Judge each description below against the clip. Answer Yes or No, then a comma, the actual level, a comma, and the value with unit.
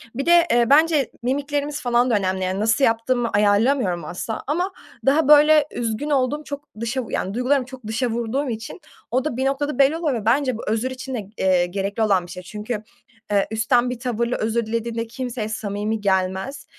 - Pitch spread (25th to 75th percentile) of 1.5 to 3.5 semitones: No, average, 4.3 semitones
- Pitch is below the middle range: No, high, 240 Hz